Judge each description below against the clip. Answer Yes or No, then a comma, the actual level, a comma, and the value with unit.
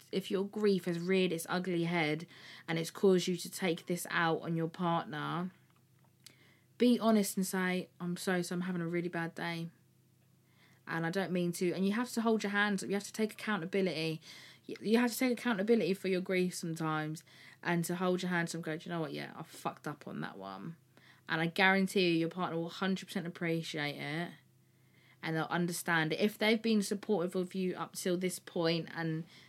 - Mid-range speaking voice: Yes, medium, 180 Hz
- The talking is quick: Yes, fast, 210 wpm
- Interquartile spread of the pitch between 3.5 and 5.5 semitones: No, average, 2.7 semitones